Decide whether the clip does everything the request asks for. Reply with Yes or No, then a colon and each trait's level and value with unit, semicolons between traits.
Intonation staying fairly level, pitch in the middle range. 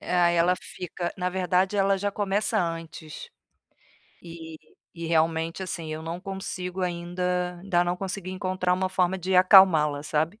Yes: narrow, 2.0 semitones; medium, 180 Hz